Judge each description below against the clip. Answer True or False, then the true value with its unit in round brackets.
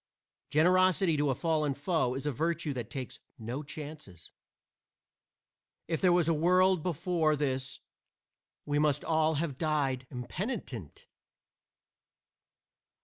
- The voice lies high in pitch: False (150 Hz)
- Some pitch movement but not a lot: True (3.9 semitones)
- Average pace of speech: False (115 wpm)